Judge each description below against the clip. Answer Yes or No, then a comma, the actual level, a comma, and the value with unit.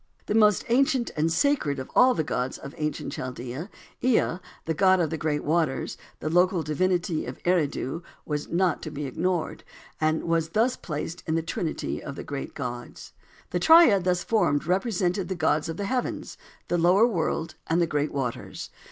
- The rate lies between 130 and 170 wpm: No, average, 180 wpm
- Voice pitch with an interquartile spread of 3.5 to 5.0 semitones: Yes, average, 3.8 semitones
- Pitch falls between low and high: Yes, medium, 165 Hz